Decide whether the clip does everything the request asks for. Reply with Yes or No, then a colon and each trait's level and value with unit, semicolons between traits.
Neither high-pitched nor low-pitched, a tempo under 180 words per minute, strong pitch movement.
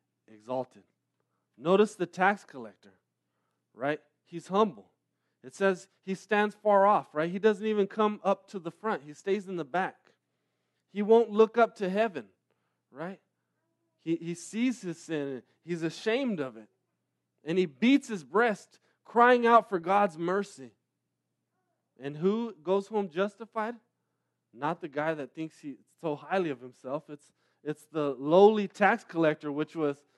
Yes: medium, 175 Hz; average, 155 wpm; wide, 6.4 semitones